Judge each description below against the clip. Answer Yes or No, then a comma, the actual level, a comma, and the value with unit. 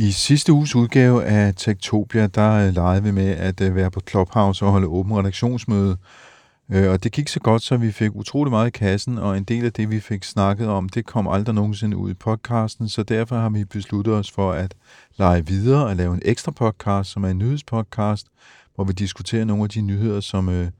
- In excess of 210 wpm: Yes, average, 220 wpm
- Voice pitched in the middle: No, low, 105 Hz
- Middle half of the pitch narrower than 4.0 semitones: Yes, narrow, 2.6 semitones